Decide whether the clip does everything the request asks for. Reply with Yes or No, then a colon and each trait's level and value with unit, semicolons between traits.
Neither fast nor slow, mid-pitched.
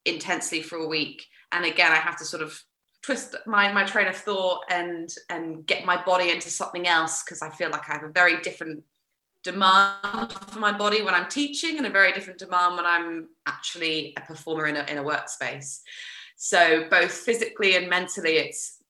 Yes: average, 195 wpm; medium, 175 Hz